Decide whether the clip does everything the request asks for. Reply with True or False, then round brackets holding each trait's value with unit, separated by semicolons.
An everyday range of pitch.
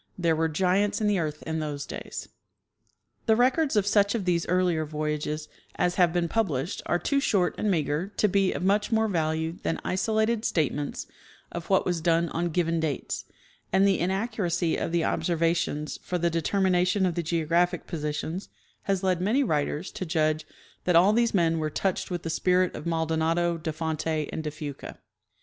True (3.2 semitones)